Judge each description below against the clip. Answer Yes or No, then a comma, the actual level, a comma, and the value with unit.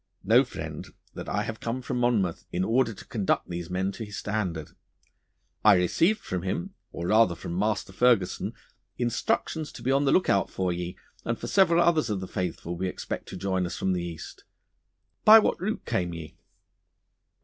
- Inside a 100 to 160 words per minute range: No, average, 185 wpm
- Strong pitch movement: Yes, wide, 5.7 semitones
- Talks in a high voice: No, low, 100 Hz